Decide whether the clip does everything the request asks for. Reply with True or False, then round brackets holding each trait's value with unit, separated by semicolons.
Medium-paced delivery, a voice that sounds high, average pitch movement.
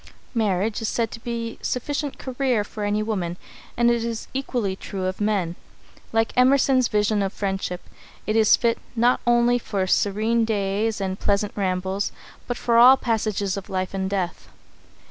True (165 wpm; 215 Hz; 3.3 semitones)